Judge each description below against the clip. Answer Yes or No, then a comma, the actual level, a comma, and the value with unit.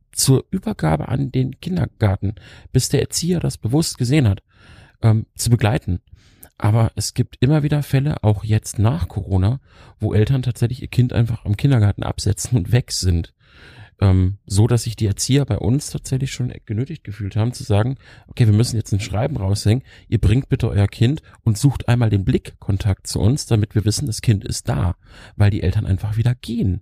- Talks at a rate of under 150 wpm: No, fast, 190 wpm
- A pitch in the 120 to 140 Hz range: No, low, 110 Hz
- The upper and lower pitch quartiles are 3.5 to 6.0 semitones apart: Yes, average, 3.8 semitones